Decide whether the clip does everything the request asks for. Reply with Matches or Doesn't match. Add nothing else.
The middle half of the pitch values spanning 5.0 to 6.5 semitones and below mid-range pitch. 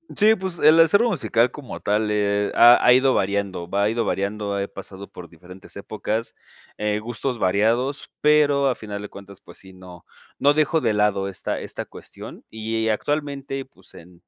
Matches